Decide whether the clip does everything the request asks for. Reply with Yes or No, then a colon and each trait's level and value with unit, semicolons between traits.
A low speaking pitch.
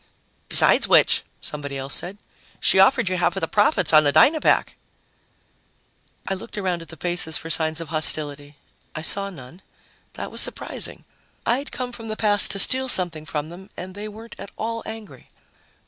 No: medium, 185 Hz